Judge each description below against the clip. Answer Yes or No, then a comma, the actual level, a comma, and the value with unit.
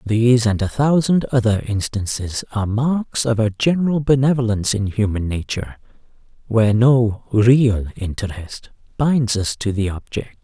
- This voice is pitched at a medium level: No, low, 115 Hz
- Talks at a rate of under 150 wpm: Yes, average, 140 wpm